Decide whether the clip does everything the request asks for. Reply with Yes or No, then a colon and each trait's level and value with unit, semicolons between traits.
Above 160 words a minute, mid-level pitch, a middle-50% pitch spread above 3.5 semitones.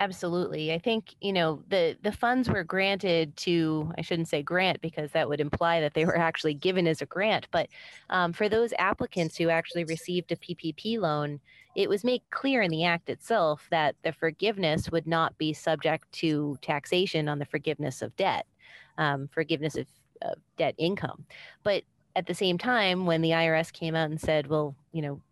No: average, 190 wpm; medium, 165 Hz; average, 2.9 semitones